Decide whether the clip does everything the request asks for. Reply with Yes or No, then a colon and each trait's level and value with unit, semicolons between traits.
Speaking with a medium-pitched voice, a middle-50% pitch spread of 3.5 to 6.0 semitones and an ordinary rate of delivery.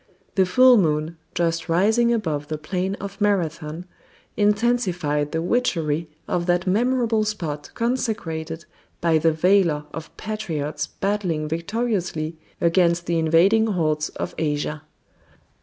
No: medium, 175 Hz; average, 4.8 semitones; slow, 120 wpm